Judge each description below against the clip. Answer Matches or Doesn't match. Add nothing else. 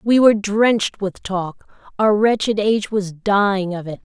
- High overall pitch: Matches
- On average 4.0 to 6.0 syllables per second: Matches